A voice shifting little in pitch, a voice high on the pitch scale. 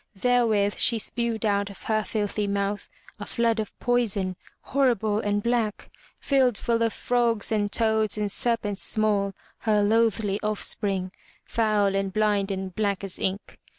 Yes: narrow, 2.3 semitones; high, 210 Hz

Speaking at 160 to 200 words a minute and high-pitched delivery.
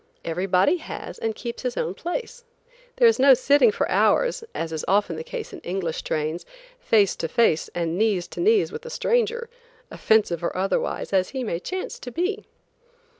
Yes: average, 180 wpm; high, 225 Hz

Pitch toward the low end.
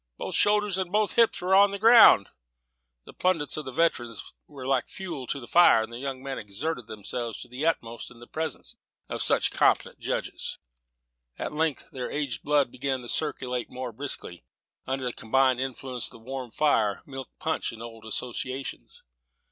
Yes: low, 130 Hz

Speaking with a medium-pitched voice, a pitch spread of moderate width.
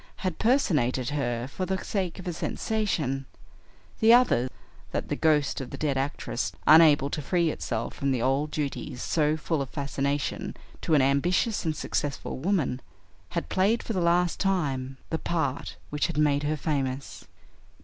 Yes: medium, 150 Hz; average, 4.3 semitones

